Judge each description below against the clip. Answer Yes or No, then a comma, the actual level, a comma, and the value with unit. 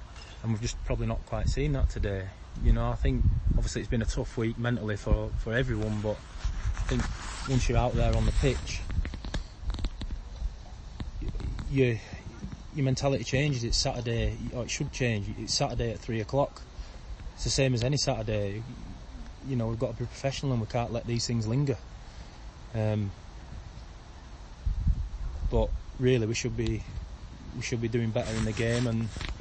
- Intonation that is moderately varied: Yes, average, 4.2 semitones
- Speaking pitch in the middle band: No, low, 115 Hz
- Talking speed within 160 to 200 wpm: Yes, average, 170 wpm